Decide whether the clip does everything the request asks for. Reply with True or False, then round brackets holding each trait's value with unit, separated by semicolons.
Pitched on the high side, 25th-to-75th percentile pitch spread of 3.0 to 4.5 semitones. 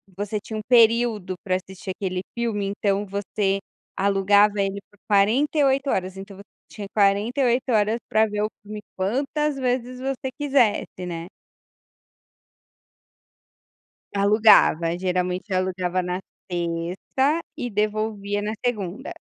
True (205 Hz; 3.7 semitones)